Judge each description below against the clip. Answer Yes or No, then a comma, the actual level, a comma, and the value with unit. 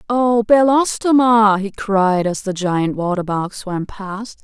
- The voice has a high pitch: Yes, high, 210 Hz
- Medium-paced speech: Yes, average, 150 wpm